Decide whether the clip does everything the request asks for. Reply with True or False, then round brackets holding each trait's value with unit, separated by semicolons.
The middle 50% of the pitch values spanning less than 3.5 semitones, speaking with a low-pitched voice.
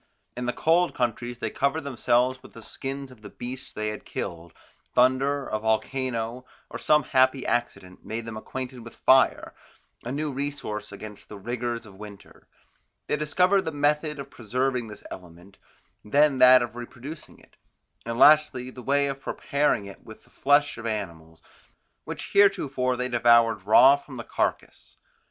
False (3.9 semitones; 125 Hz)